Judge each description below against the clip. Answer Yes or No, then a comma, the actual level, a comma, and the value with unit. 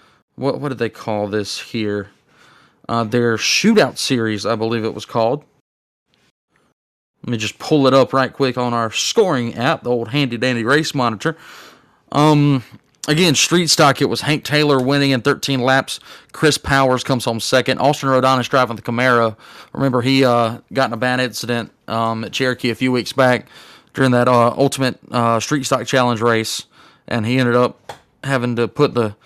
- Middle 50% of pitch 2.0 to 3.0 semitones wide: Yes, narrow, 2.6 semitones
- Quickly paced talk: No, average, 185 wpm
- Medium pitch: No, low, 125 Hz